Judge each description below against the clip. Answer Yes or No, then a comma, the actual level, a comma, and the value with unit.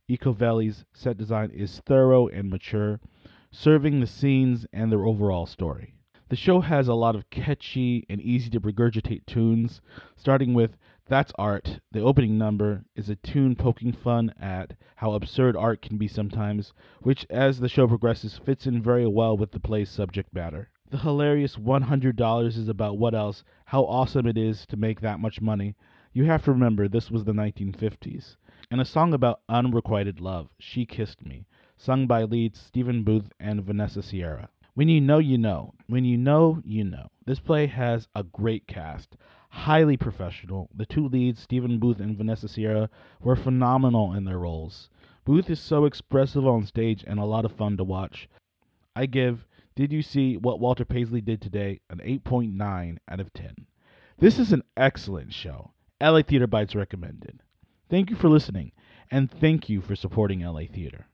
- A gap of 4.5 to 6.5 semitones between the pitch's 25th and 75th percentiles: No, average, 3.8 semitones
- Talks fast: No, average, 175 wpm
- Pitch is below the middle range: Yes, low, 115 Hz